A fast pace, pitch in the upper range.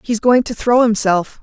Yes: fast, 210 wpm; high, 225 Hz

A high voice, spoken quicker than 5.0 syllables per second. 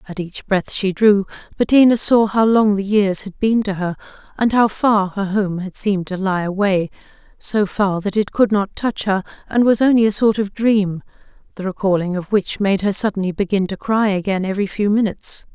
Yes: high, 200 Hz; 5.2 syllables/s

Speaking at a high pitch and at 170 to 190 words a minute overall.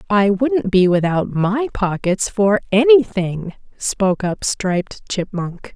No: high, 205 Hz; slow, 135 wpm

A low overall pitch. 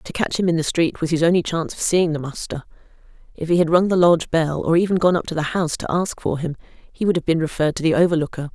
No: medium, 165 Hz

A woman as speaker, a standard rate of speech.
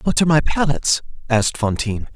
No: male; average, 165 wpm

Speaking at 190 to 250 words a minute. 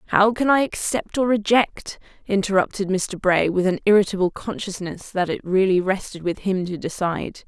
No: average, 170 wpm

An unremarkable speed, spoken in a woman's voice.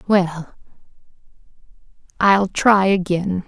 No: slow, 70 wpm; female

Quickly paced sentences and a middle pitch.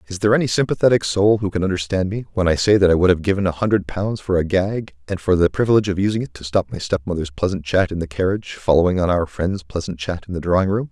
No: fast, 270 wpm; very low, 95 Hz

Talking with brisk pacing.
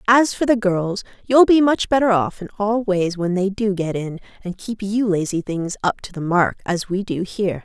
Yes: fast, 235 wpm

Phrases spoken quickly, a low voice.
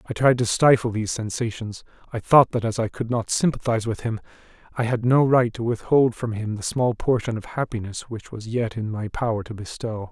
Yes: fast, 220 wpm; low, 115 Hz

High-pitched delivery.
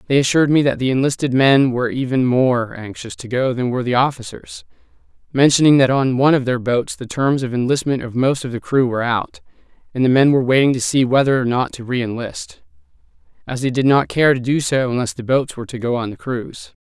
No: low, 130 Hz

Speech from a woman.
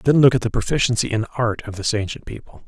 No: male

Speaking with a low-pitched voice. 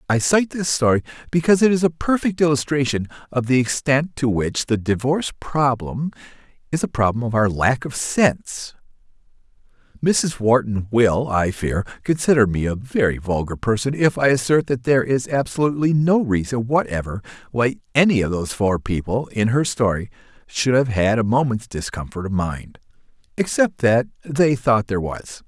Yes: low, 125 Hz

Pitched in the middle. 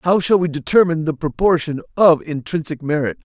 Yes: medium, 160 Hz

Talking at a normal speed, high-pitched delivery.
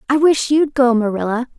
Yes: average, 190 wpm; very high, 260 Hz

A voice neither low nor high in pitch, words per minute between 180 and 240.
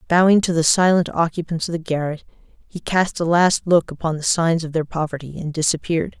Yes: medium, 165 Hz; fast, 205 wpm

